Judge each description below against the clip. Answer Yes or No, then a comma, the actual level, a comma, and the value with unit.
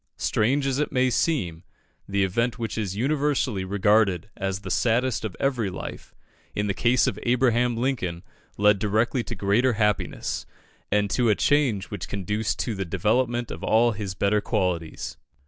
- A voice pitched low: Yes, low, 110 Hz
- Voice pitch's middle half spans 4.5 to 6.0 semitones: No, average, 3.8 semitones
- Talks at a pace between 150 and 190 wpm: Yes, average, 165 wpm